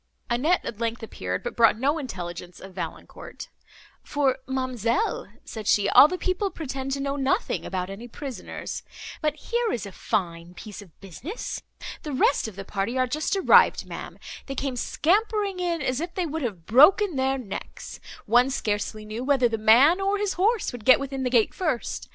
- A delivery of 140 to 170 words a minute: No, average, 185 wpm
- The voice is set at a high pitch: Yes, very high, 260 Hz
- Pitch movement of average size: No, wide, 6.8 semitones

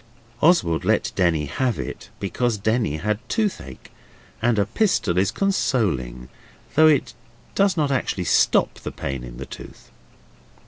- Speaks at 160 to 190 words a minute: No, average, 140 wpm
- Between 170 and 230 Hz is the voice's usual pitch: No, low, 105 Hz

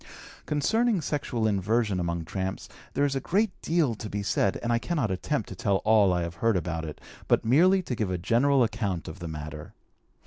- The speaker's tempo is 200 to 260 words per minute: Yes, fast, 205 wpm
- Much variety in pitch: Yes, wide, 7.5 semitones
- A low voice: Yes, low, 110 Hz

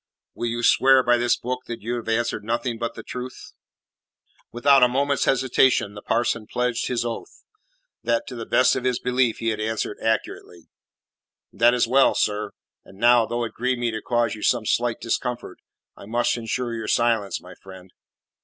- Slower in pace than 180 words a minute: No, average, 185 wpm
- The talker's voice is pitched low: Yes, low, 120 Hz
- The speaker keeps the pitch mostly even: Yes, narrow, 1.7 semitones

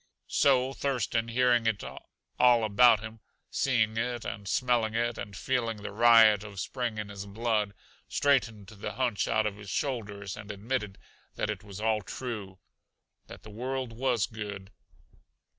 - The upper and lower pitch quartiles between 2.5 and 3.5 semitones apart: Yes, average, 3.0 semitones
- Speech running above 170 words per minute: No, average, 155 wpm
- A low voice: Yes, low, 110 Hz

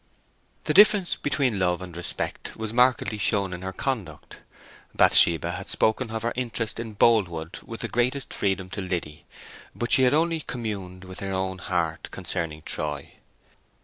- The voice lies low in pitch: Yes, low, 100 Hz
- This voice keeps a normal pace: Yes, average, 160 wpm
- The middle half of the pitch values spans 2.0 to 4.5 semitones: No, average, 5.0 semitones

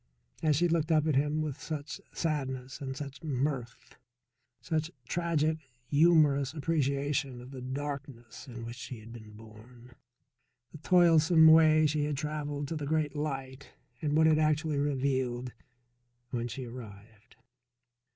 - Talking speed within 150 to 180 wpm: No, average, 140 wpm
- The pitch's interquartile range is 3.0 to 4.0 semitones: Yes, average, 3.4 semitones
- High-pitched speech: No, medium, 145 Hz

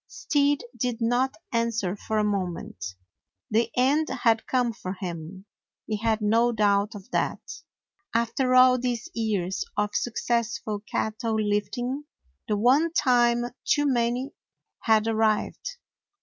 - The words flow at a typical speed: No, slow, 130 wpm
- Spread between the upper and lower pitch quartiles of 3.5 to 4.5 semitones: No, average, 3.1 semitones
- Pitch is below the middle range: No, high, 230 Hz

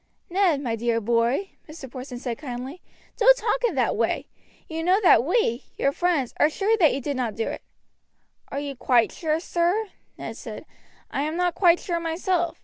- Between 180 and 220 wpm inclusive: Yes, average, 190 wpm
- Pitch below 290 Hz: No, very high, 305 Hz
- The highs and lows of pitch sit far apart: Yes, wide, 6.1 semitones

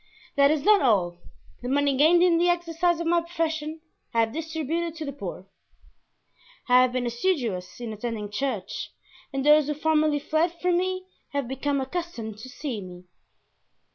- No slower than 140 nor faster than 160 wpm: No, average, 170 wpm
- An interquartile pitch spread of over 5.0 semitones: Yes, wide, 5.4 semitones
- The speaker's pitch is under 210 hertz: No, very high, 290 Hz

